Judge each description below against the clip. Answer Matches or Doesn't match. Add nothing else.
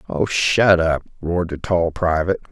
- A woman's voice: Doesn't match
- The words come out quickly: Doesn't match